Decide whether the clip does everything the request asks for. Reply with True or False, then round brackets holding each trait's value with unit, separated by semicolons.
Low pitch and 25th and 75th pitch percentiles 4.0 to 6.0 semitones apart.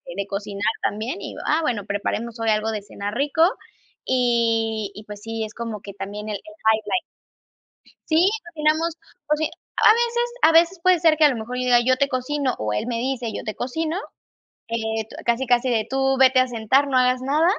False (245 Hz; 5.1 semitones)